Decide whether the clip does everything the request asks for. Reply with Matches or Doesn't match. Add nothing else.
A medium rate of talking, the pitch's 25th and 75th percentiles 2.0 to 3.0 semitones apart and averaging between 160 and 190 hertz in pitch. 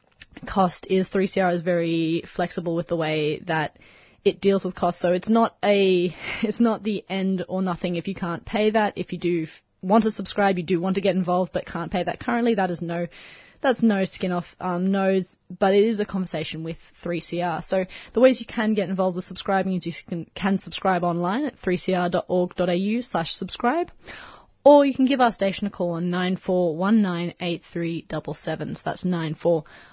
Matches